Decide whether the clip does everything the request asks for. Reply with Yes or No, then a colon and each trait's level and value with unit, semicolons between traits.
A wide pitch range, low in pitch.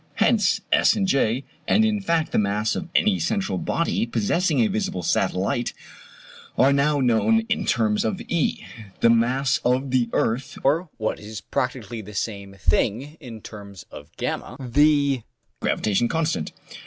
Yes: wide, 6.1 semitones; low, 125 Hz